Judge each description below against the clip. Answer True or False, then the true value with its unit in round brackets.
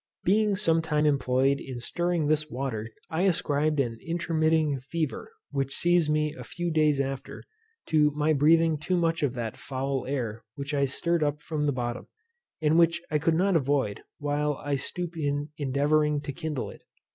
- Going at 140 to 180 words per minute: True (175 wpm)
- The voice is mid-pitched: True (150 Hz)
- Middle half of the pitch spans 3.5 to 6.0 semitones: False (2.8 semitones)